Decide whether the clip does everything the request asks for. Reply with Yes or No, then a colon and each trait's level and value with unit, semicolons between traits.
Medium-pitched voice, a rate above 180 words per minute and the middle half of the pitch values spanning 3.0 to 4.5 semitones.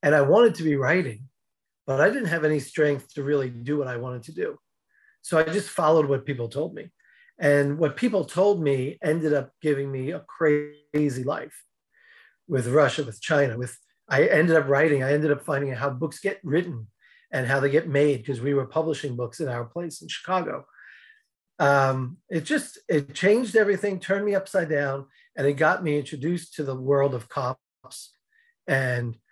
Yes: medium, 150 Hz; average, 190 wpm; average, 4.0 semitones